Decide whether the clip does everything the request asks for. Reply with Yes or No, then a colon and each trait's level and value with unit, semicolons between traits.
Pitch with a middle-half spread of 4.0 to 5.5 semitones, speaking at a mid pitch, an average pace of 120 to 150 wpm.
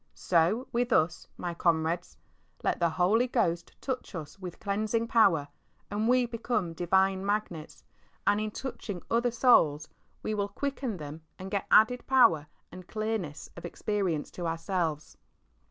No: average, 5.2 semitones; high, 195 Hz; average, 145 wpm